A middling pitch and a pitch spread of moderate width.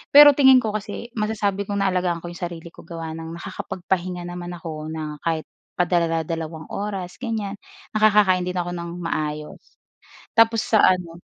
Yes: medium, 180 Hz; average, 3.5 semitones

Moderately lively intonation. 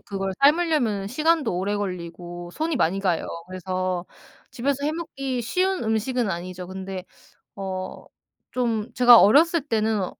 No: wide, 6.7 semitones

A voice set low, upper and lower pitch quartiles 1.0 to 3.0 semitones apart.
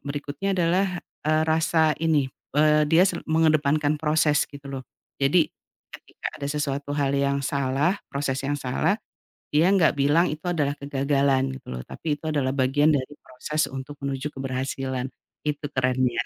No: medium, 145 Hz; narrow, 2.4 semitones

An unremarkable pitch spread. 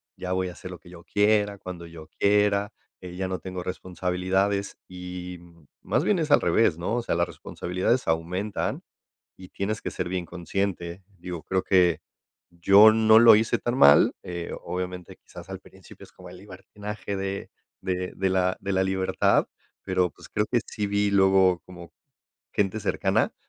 No: narrow, 2.1 semitones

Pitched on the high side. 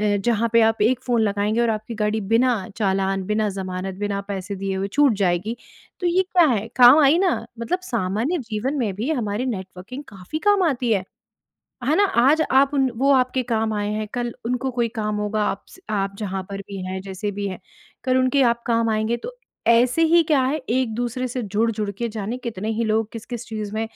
Yes: high, 225 Hz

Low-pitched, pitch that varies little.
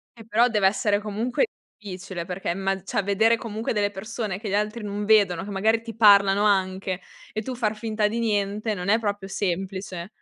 No: high, 205 Hz; narrow, 2.2 semitones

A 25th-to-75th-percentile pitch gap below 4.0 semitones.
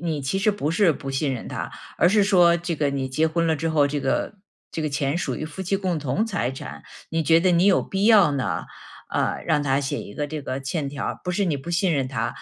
No: average, 4.3 semitones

